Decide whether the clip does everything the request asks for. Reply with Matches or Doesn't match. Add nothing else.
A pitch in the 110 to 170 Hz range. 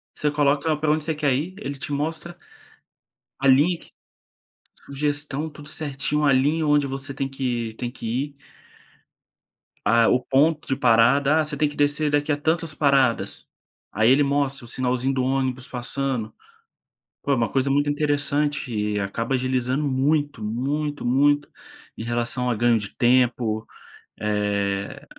Matches